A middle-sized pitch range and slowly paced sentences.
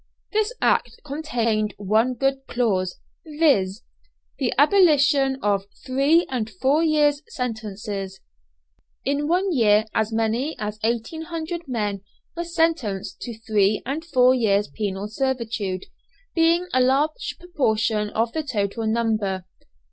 No: wide, 5.8 semitones; slow, 120 wpm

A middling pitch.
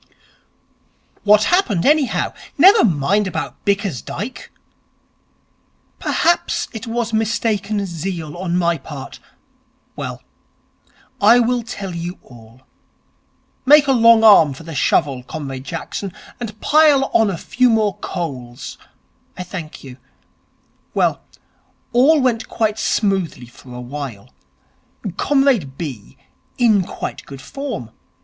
No: high, 195 Hz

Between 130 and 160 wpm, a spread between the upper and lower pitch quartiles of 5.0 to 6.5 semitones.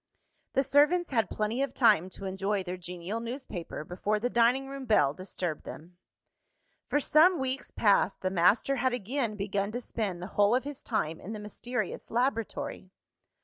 No: average, 170 wpm; wide, 5.5 semitones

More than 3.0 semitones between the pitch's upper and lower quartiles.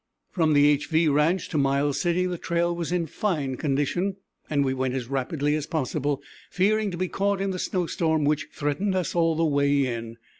Yes: average, 3.8 semitones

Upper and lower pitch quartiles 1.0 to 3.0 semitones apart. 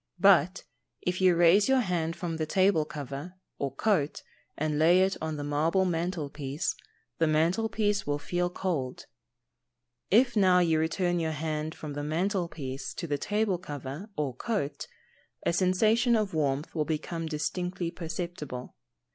No: average, 3.7 semitones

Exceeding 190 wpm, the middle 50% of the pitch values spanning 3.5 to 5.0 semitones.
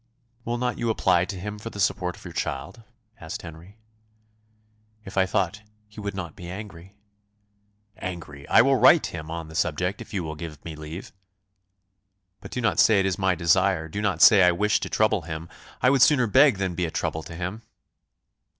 Yes: fast, 205 wpm; average, 4.0 semitones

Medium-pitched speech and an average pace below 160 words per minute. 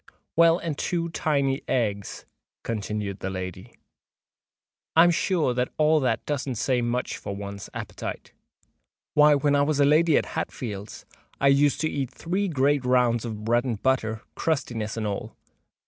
No: low, 130 Hz; average, 145 wpm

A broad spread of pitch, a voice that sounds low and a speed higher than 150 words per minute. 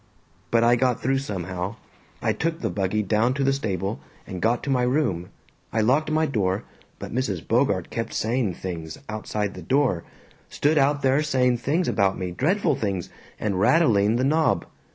Yes: wide, 5.8 semitones; low, 120 Hz; average, 175 wpm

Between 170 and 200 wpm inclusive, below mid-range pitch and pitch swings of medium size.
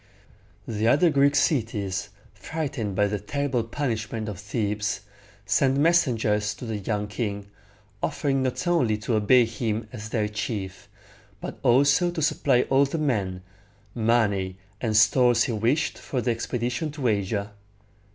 No: average, 140 wpm; low, 115 Hz; average, 4.4 semitones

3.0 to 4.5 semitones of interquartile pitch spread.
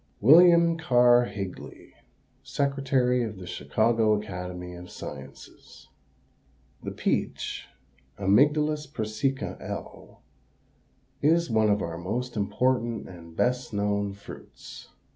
No: average, 5.1 semitones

